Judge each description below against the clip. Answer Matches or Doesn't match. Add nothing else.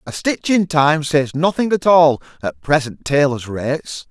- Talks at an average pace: Matches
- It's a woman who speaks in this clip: Doesn't match